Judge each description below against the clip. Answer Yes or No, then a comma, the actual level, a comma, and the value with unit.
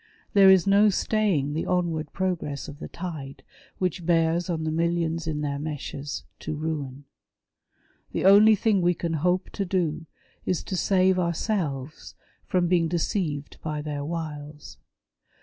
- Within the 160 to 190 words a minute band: No, average, 150 wpm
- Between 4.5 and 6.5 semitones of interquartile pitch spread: No, average, 3.5 semitones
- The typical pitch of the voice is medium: Yes, medium, 165 Hz